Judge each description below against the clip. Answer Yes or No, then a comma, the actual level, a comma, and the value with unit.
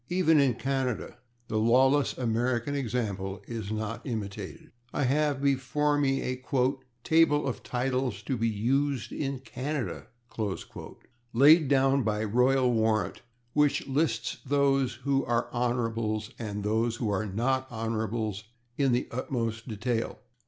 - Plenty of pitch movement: No, average, 3.5 semitones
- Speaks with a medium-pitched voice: No, low, 125 Hz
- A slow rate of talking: Yes, slow, 130 wpm